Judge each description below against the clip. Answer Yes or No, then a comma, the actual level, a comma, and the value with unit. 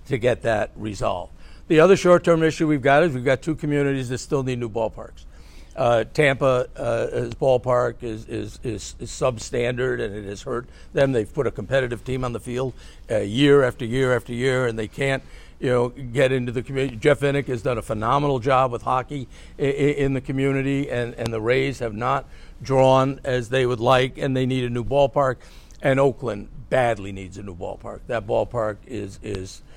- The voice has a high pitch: No, low, 130 Hz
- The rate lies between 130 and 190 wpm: No, average, 200 wpm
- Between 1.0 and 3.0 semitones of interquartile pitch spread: Yes, narrow, 2.6 semitones